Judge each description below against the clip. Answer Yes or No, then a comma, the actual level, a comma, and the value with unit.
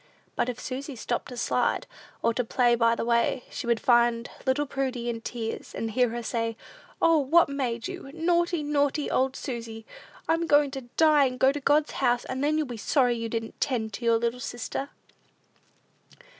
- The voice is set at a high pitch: Yes, very high, 250 Hz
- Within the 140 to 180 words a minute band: No, average, 190 wpm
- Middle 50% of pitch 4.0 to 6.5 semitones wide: No, average, 3.4 semitones